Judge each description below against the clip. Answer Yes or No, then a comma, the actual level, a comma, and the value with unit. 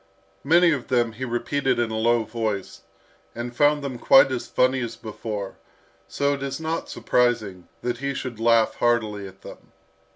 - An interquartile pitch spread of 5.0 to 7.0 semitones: No, average, 3.3 semitones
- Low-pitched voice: Yes, low, 120 Hz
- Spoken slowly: No, average, 170 wpm